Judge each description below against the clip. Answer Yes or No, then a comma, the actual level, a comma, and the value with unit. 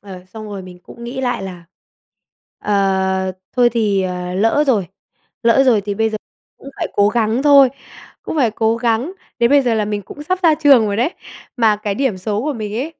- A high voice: Yes, high, 220 Hz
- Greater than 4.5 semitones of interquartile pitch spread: No, average, 4.1 semitones